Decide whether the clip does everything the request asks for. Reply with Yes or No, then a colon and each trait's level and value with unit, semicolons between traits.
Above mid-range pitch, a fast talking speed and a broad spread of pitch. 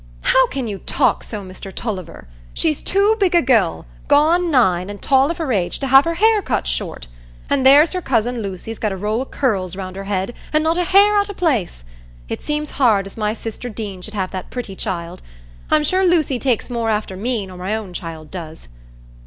Yes: high, 225 Hz; fast, 210 wpm; wide, 7.8 semitones